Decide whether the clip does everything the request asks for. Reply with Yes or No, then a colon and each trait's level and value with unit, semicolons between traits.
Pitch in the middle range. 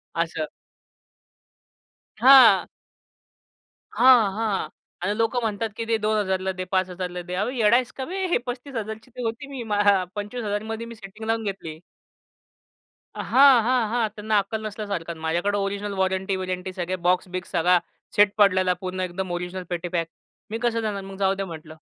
No: high, 200 Hz